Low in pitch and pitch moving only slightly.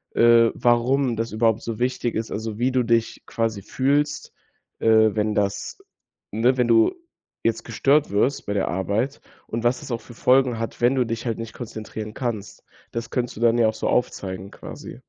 Yes: low, 115 Hz; narrow, 2.1 semitones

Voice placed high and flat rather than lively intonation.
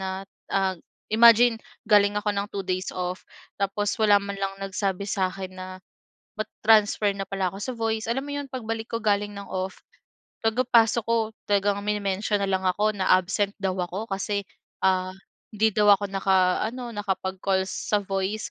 Yes: high, 200 Hz; narrow, 2.2 semitones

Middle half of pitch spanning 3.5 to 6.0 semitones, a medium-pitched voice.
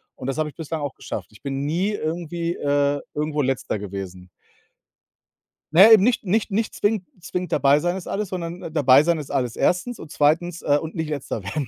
Yes: average, 3.9 semitones; medium, 155 Hz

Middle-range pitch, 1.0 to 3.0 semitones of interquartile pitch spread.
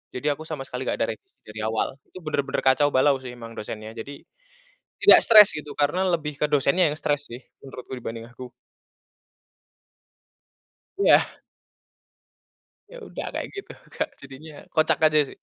No: medium, 145 Hz; average, 4.0 semitones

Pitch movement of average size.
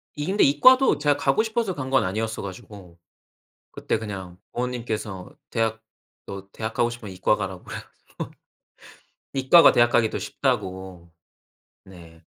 No: wide, 6.2 semitones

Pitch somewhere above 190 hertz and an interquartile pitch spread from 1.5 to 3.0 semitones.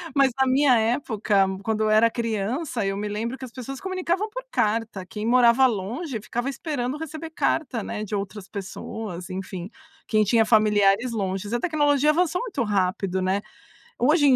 No: high, 230 Hz; average, 5.0 semitones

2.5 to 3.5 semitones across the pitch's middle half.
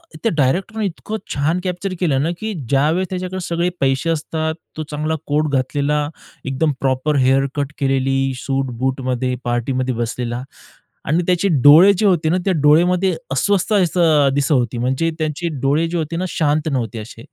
No: average, 4.5 semitones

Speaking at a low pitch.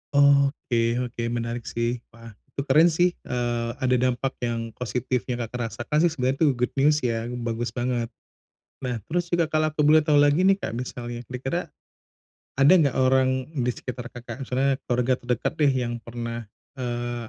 Yes: low, 125 Hz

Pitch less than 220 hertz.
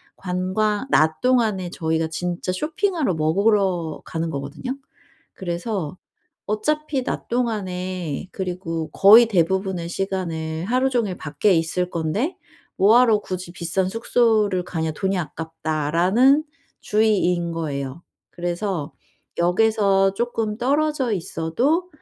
Yes: medium, 185 Hz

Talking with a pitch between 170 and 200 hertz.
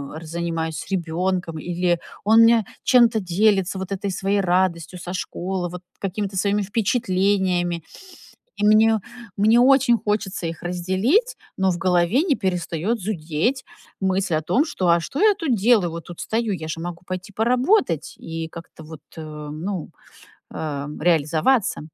Yes: medium, 185 Hz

